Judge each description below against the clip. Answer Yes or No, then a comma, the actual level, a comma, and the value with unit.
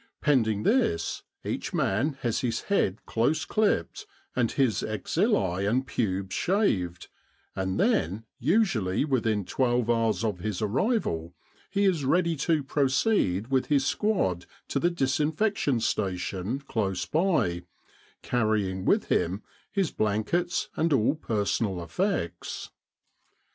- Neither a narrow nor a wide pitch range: No, wide, 8.3 semitones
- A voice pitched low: Yes, low, 115 Hz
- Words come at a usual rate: No, slow, 120 wpm